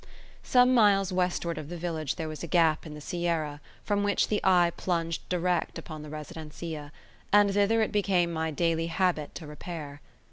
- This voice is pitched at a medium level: Yes, medium, 170 Hz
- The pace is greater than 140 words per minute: Yes, average, 180 wpm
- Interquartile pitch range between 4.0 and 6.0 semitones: No, average, 3.3 semitones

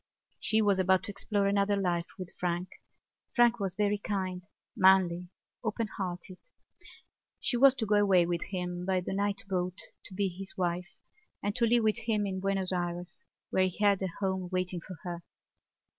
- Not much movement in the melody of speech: Yes, narrow, 2.2 semitones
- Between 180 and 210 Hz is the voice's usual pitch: Yes, high, 190 Hz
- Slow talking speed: No, average, 175 wpm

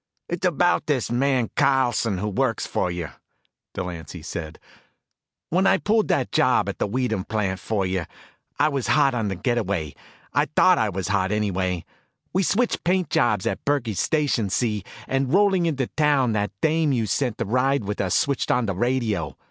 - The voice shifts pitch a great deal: Yes, wide, 6.5 semitones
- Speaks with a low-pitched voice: Yes, low, 120 Hz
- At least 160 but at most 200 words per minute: Yes, average, 180 wpm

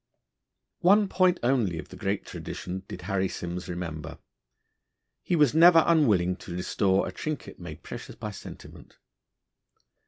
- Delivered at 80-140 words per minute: Yes, slow, 135 wpm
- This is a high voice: No, low, 100 Hz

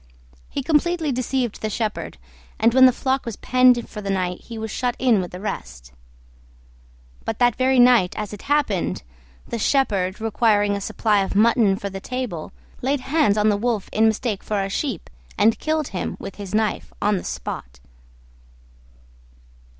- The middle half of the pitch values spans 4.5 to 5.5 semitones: No, average, 4.1 semitones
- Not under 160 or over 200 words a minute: Yes, average, 175 wpm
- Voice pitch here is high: Yes, high, 220 Hz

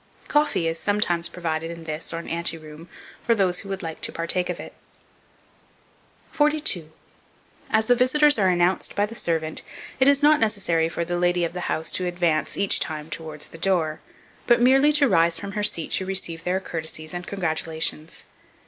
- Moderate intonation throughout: Yes, average, 4.1 semitones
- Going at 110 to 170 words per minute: No, average, 185 wpm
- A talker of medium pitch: Yes, medium, 175 Hz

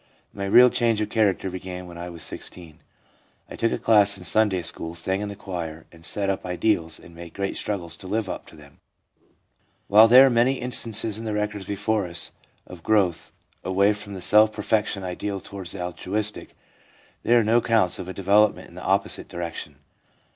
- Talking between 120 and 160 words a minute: No, average, 195 wpm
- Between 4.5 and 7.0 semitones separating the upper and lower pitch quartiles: No, average, 3.2 semitones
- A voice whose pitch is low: Yes, low, 100 Hz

